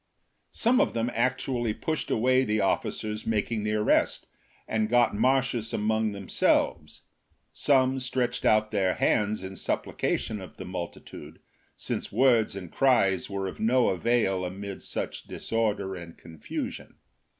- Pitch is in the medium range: No, low, 110 Hz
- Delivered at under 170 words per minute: Yes, average, 140 wpm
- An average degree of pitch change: Yes, average, 3.9 semitones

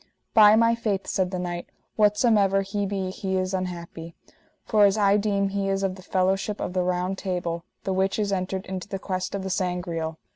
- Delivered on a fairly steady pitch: Yes, narrow, 1.6 semitones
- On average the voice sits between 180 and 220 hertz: Yes, high, 190 Hz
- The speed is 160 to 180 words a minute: No, fast, 205 wpm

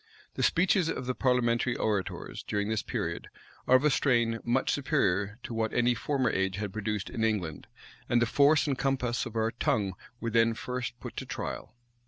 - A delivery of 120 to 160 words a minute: No, average, 190 wpm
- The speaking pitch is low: Yes, low, 115 Hz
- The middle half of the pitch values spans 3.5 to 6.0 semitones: No, average, 3.0 semitones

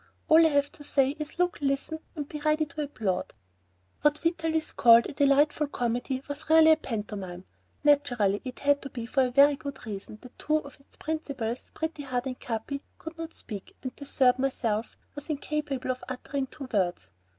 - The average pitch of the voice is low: No, very high, 275 Hz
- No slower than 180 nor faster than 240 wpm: Yes, average, 190 wpm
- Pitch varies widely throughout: No, average, 3.6 semitones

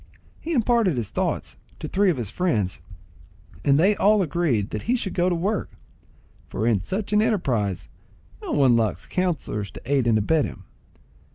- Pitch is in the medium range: Yes, medium, 160 Hz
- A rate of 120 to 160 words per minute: No, average, 175 wpm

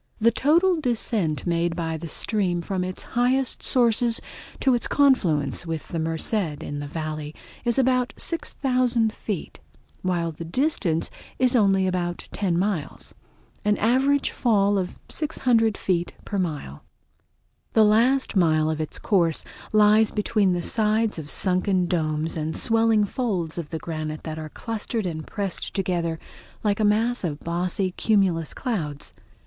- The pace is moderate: Yes, average, 145 wpm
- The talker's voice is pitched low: No, high, 195 Hz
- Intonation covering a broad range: Yes, wide, 5.7 semitones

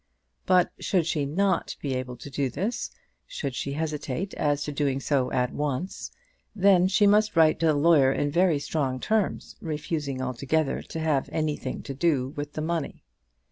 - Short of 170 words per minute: No, average, 175 wpm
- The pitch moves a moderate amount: Yes, average, 3.7 semitones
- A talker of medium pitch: Yes, medium, 150 Hz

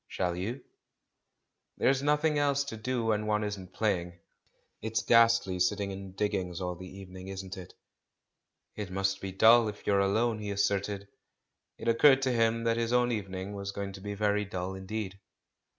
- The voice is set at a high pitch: No, low, 100 Hz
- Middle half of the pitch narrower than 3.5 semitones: Yes, average, 3.1 semitones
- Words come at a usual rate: Yes, average, 170 wpm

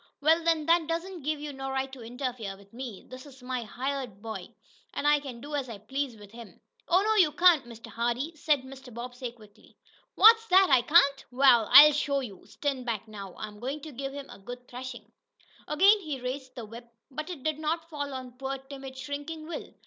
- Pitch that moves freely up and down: No, average, 3.9 semitones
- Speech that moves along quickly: Yes, fast, 210 wpm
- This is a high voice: Yes, very high, 270 Hz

